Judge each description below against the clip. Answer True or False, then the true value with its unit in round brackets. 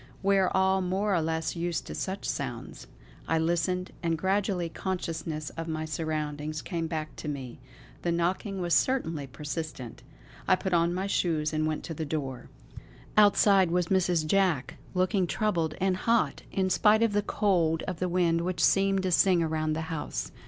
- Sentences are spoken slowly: False (175 wpm)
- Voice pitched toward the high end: False (170 Hz)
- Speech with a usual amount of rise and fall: True (3.1 semitones)